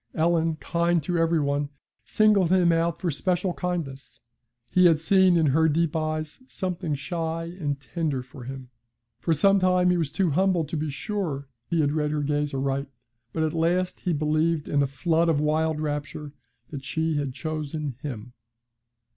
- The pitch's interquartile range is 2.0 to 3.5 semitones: Yes, average, 2.8 semitones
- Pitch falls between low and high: Yes, medium, 160 Hz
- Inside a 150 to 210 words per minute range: Yes, average, 175 wpm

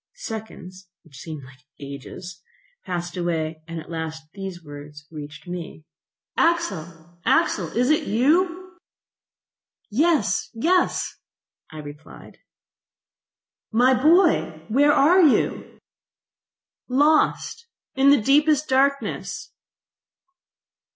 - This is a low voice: No, high, 200 Hz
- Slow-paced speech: Yes, slow, 90 wpm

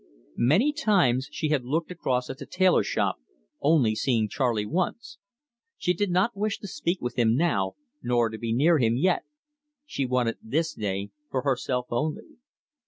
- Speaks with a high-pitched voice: No, low, 135 Hz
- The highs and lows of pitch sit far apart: Yes, wide, 6.8 semitones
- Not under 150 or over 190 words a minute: Yes, average, 170 wpm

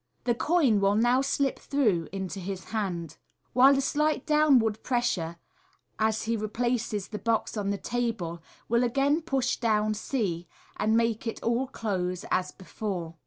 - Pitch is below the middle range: No, high, 225 Hz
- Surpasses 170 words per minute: No, average, 150 wpm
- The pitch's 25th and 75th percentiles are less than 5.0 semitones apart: Yes, average, 4.2 semitones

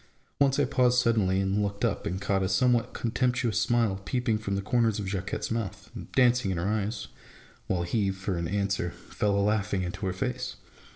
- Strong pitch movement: No, average, 3.8 semitones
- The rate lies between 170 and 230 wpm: Yes, average, 195 wpm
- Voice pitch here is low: Yes, low, 105 Hz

